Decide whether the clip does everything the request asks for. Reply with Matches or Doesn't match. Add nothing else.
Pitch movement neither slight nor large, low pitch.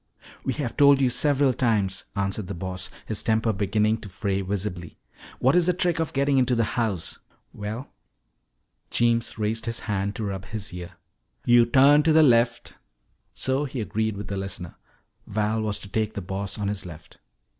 Matches